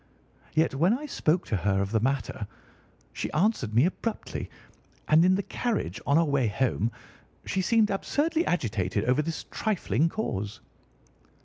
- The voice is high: No, medium, 155 Hz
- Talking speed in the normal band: Yes, average, 150 wpm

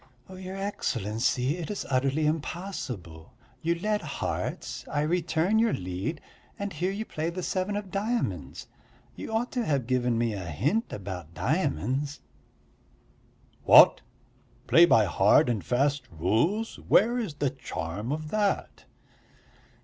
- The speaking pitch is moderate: Yes, medium, 150 Hz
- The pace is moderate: No, slow, 130 wpm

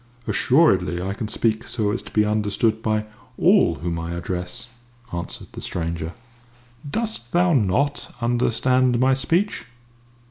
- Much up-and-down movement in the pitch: Yes, wide, 6.2 semitones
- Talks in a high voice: No, low, 110 Hz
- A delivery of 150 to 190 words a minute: No, slow, 135 wpm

